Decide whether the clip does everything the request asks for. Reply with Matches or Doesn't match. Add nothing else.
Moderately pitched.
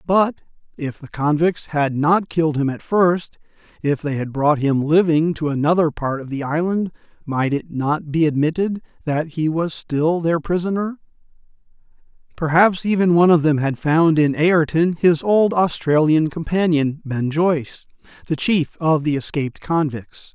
Matches